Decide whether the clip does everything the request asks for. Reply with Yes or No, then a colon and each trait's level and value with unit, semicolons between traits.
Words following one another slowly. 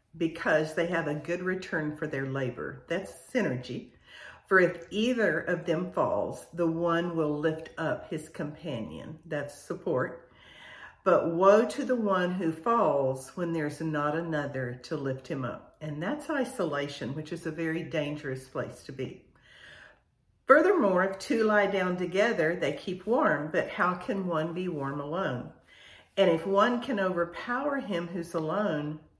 No: average, 155 wpm